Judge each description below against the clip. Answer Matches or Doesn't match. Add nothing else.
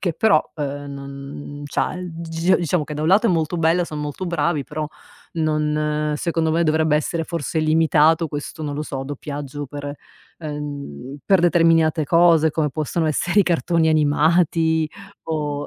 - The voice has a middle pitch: Matches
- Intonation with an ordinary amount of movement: Doesn't match